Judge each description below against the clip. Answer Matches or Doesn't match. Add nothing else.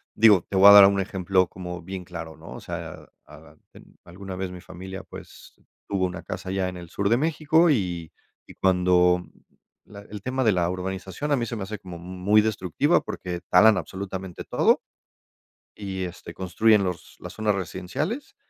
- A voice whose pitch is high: Doesn't match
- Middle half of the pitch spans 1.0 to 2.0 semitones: Doesn't match